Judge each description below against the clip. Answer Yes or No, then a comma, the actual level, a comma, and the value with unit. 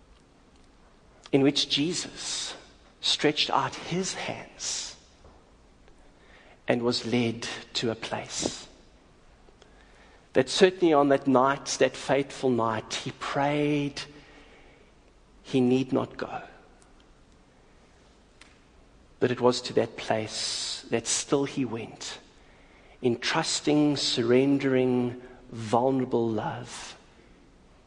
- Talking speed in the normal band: No, slow, 90 wpm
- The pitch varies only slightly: No, average, 3.7 semitones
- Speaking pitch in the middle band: No, low, 125 Hz